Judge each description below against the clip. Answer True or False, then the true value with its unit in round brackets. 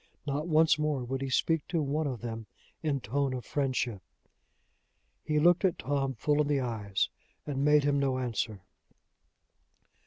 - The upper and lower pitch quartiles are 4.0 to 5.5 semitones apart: False (3.1 semitones)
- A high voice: False (140 Hz)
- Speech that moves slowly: False (160 wpm)